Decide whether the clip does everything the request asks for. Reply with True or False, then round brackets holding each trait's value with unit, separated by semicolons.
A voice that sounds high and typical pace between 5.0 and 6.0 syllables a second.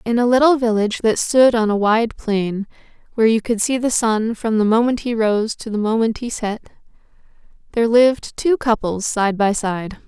True (225 Hz; 5.1 syllables/s)